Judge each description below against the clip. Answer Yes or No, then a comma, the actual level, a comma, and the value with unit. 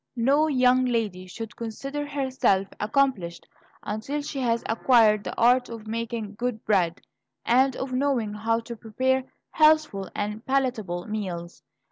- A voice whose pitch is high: Yes, high, 230 Hz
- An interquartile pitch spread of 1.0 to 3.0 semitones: No, average, 3.7 semitones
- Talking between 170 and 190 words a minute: No, slow, 135 wpm